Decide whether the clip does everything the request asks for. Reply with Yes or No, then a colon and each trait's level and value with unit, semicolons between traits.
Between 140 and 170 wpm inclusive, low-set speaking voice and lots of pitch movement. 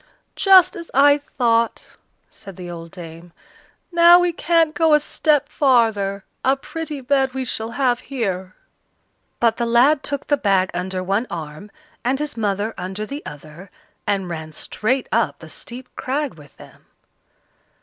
No: average, 155 wpm; high, 235 Hz; wide, 7.2 semitones